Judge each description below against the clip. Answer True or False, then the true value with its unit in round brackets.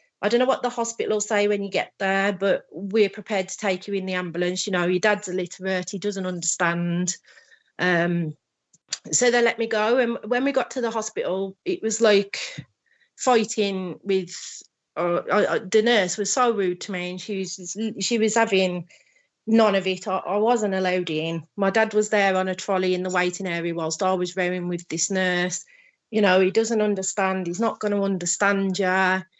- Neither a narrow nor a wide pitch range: True (3.0 semitones)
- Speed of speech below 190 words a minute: False (200 wpm)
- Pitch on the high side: True (195 Hz)